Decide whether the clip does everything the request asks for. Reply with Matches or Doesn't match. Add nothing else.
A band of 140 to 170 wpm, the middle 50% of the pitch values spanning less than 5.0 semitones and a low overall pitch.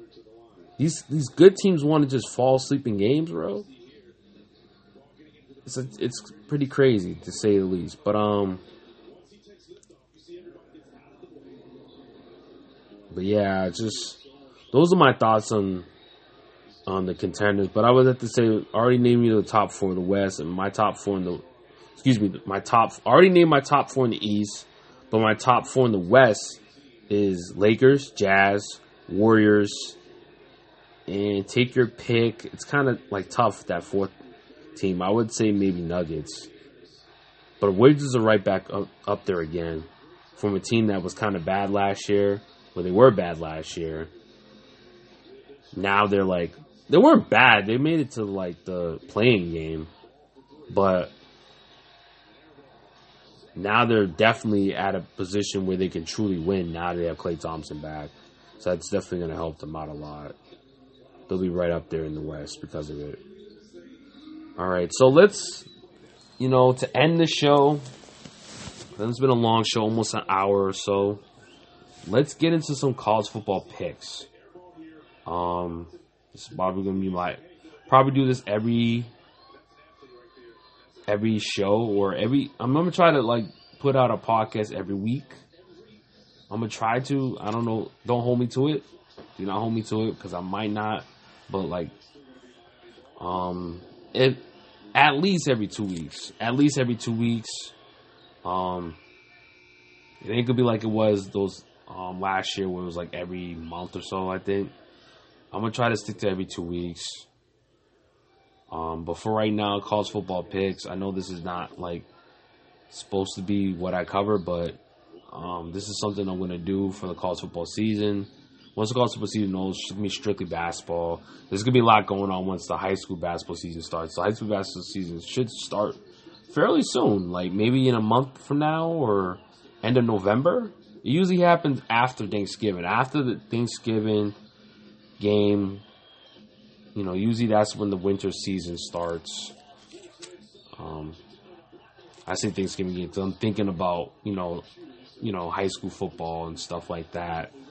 Matches